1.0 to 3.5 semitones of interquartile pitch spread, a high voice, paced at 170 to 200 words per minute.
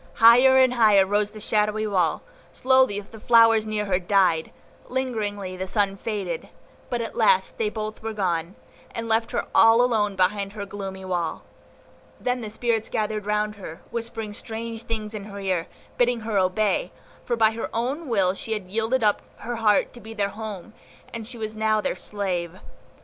Yes: narrow, 2.4 semitones; high, 215 Hz; average, 180 wpm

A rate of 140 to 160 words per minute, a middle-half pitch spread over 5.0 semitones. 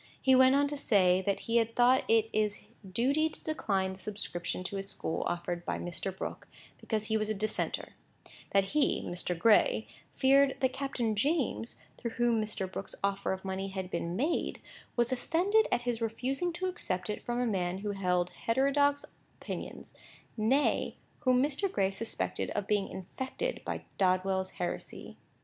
No: average, 170 wpm; wide, 5.6 semitones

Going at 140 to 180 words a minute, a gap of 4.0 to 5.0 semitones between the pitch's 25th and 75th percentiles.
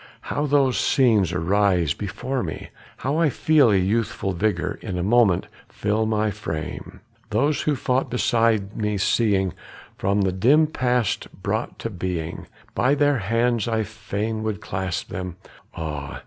Yes: average, 150 wpm; average, 4.6 semitones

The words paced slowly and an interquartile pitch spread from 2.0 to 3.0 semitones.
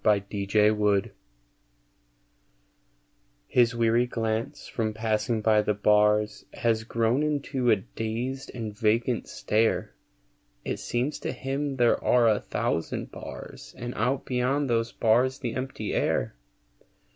Yes: slow, 120 wpm; average, 2.7 semitones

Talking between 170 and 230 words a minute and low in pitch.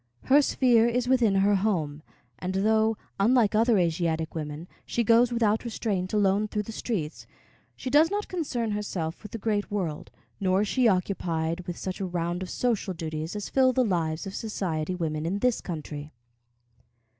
No: average, 175 wpm; high, 200 Hz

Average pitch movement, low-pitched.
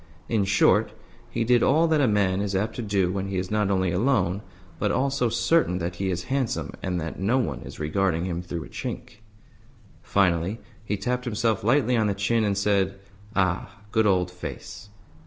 Yes: average, 4.0 semitones; low, 100 Hz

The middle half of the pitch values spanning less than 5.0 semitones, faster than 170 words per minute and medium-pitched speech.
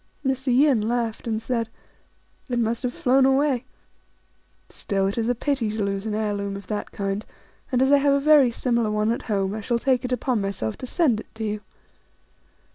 No: average, 3.5 semitones; fast, 205 wpm; high, 230 Hz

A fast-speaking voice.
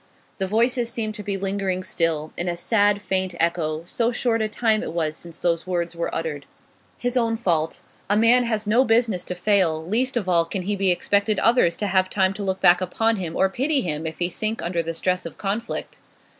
Yes: fast, 215 wpm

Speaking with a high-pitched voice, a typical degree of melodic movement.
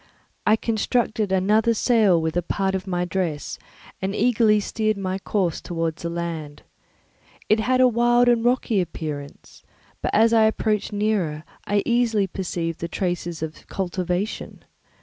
Yes: high, 195 Hz; average, 4.3 semitones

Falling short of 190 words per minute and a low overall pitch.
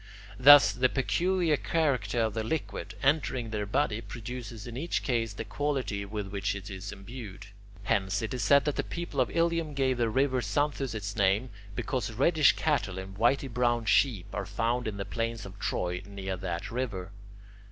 Yes: average, 180 wpm; low, 115 Hz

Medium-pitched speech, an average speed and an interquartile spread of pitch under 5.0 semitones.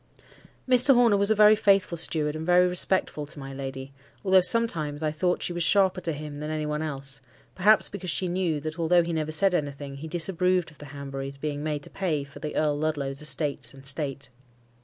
No: medium, 155 Hz; fast, 215 wpm; average, 4.0 semitones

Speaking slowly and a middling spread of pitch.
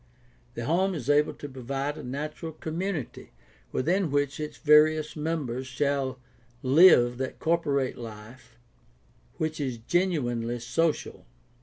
Yes: slow, 125 wpm; average, 3.9 semitones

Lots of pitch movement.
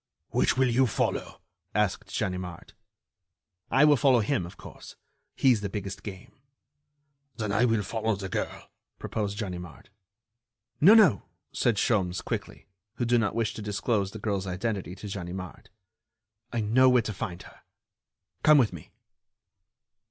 No: average, 3.9 semitones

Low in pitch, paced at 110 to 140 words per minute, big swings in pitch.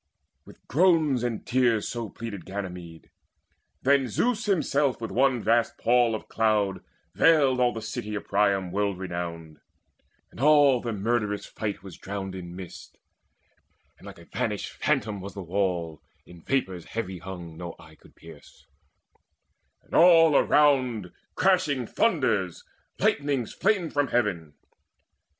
Yes: low, 110 Hz; slow, 135 wpm; wide, 6.3 semitones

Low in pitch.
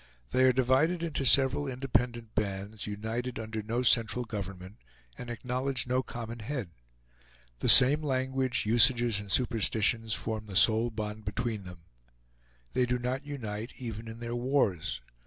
Yes: low, 120 Hz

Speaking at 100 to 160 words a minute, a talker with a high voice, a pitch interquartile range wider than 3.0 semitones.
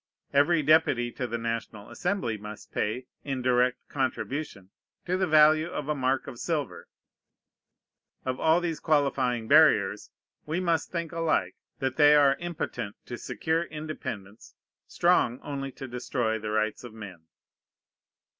No: average, 140 wpm; low, 135 Hz; average, 5.0 semitones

